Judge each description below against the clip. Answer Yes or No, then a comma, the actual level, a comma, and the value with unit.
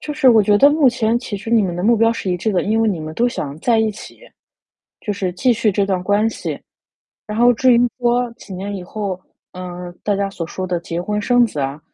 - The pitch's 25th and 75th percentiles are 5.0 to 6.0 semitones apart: No, average, 4.1 semitones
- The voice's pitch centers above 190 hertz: Yes, high, 210 Hz